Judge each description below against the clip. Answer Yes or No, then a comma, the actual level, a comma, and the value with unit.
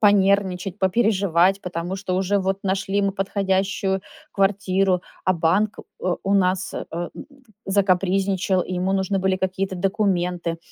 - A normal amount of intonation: No, narrow, 1.3 semitones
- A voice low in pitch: No, high, 190 Hz